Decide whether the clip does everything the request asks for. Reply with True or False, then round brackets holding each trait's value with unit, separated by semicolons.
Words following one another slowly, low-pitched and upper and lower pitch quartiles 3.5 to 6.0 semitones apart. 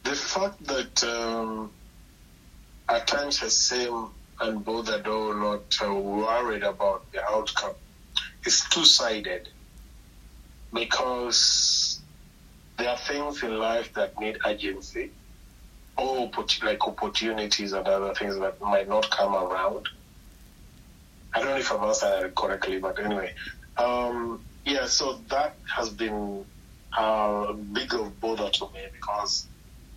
False (125 wpm; 105 Hz; 3.1 semitones)